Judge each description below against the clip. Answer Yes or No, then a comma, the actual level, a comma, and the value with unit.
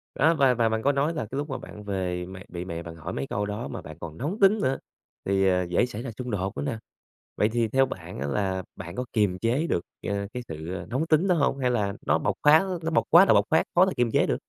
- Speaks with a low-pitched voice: Yes, low, 115 Hz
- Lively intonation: Yes, wide, 7.0 semitones